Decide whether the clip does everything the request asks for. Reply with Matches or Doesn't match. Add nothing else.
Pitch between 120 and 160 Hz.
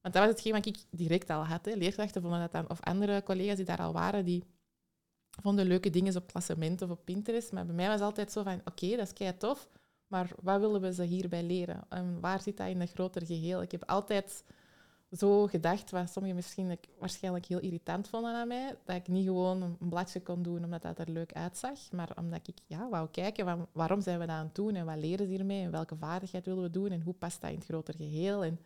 Doesn't match